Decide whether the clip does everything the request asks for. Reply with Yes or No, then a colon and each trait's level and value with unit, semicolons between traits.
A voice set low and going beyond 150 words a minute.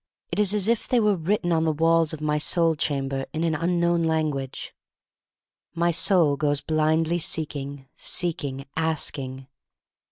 No: medium, 160 Hz; average, 160 wpm